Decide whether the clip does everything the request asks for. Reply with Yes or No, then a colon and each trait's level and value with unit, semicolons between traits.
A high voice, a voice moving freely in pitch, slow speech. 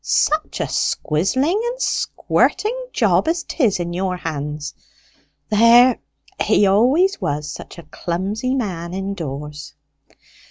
Yes: high, 195 Hz; wide, 8.2 semitones; slow, 115 wpm